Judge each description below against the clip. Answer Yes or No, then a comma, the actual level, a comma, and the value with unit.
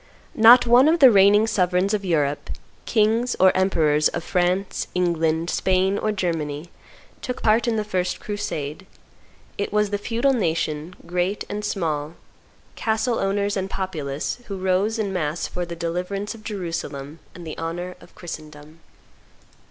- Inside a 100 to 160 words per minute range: Yes, average, 150 wpm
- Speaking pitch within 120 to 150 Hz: No, medium, 185 Hz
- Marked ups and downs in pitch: No, average, 4.0 semitones